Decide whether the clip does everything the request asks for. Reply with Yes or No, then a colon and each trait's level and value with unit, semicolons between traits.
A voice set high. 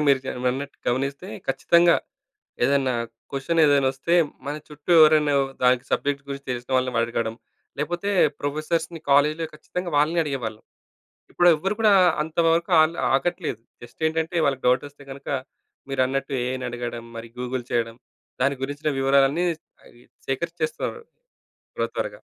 No: medium, 140 Hz